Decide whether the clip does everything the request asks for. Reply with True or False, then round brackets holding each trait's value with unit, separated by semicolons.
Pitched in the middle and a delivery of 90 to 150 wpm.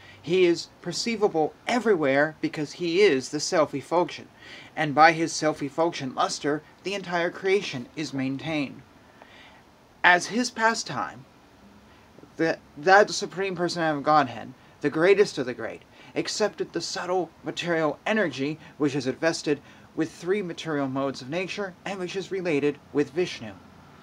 True (160 Hz; 135 wpm)